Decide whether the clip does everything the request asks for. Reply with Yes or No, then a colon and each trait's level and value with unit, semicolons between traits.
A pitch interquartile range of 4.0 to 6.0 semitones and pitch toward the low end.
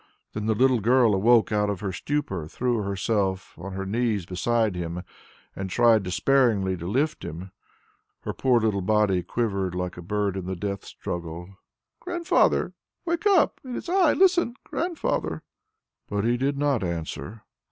Yes: average, 5.1 semitones; low, 105 Hz